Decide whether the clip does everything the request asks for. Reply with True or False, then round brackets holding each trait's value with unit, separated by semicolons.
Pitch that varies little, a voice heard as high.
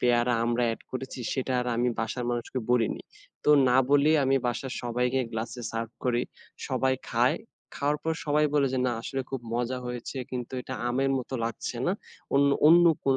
False (2.1 semitones; 125 Hz)